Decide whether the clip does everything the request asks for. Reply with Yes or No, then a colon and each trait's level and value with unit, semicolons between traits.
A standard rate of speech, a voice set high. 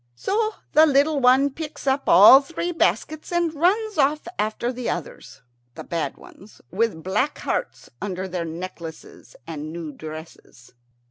Yes: average, 145 wpm; high, 245 Hz